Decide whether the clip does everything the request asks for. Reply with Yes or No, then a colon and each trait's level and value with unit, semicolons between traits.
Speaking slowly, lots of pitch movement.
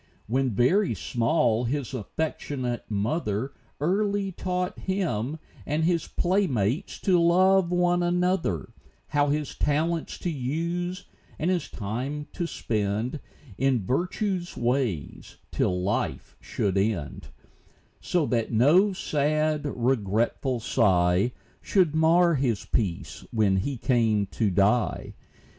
Yes: slow, 115 wpm; wide, 7.6 semitones